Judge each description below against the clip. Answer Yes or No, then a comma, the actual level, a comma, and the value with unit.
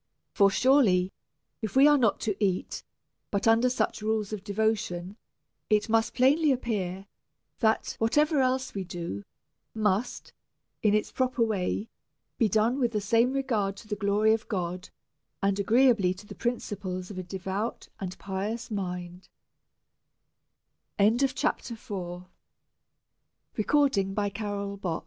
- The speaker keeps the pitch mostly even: No, average, 3.4 semitones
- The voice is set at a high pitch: Yes, high, 210 Hz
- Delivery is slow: Yes, slow, 125 wpm